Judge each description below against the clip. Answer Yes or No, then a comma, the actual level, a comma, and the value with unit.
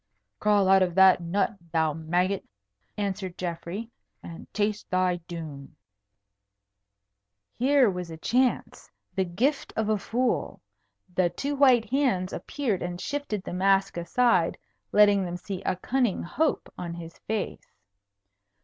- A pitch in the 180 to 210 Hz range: Yes, high, 190 Hz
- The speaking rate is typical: No, slow, 130 wpm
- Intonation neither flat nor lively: Yes, average, 4.2 semitones